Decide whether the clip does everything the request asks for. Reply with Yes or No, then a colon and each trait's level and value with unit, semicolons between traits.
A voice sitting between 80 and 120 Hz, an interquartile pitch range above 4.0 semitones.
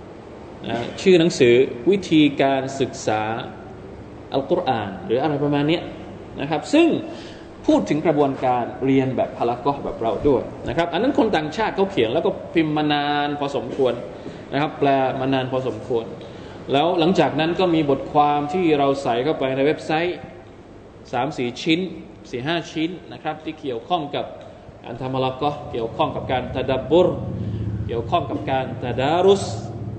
No: medium, 140 Hz; average, 4.4 semitones